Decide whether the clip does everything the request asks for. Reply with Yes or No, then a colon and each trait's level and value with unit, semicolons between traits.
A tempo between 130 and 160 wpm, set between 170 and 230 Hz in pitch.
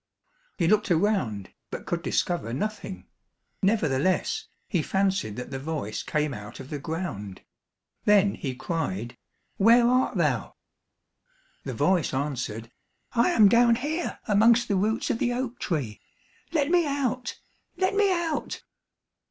Yes: slow, 135 wpm; high, 190 Hz